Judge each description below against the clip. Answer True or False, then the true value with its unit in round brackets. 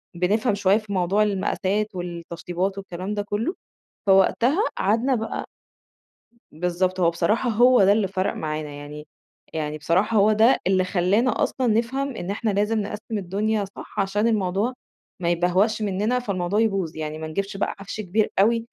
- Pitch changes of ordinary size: True (3.4 semitones)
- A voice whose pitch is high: True (200 Hz)